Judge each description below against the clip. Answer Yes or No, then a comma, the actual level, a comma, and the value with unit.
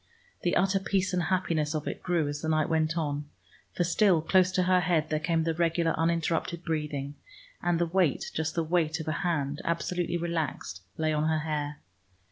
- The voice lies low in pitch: No, medium, 165 Hz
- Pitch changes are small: Yes, narrow, 2.1 semitones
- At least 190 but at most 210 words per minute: Yes, average, 195 wpm